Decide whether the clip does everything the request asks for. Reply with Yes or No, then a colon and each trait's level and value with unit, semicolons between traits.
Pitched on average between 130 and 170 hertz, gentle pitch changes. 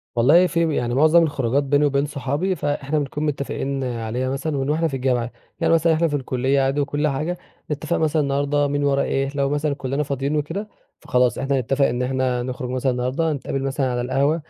Yes: medium, 140 Hz; narrow, 2.3 semitones